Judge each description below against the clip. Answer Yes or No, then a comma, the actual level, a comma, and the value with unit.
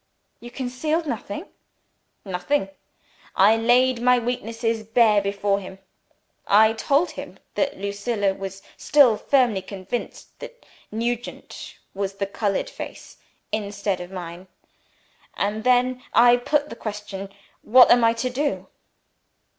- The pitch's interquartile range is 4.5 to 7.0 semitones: No, average, 3.8 semitones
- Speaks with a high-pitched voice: Yes, high, 225 Hz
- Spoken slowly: Yes, slow, 125 wpm